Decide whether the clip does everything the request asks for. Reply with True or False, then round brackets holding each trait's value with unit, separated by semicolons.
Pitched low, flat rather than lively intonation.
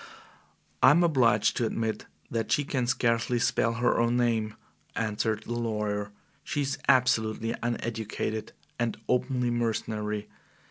True (115 Hz; 2.0 semitones)